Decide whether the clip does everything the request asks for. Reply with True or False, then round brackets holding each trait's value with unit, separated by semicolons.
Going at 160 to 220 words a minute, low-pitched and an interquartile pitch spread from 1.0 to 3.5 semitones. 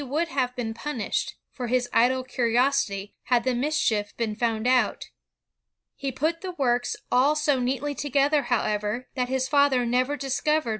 False (165 wpm; 255 Hz; 2.8 semitones)